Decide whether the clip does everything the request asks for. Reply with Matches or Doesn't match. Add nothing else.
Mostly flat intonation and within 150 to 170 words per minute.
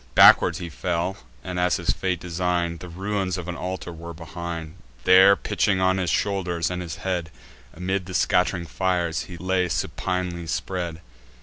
Matches